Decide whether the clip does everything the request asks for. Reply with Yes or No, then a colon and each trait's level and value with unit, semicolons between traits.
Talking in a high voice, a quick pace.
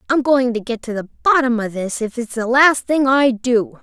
Yes: high, 245 Hz; fast, 250 wpm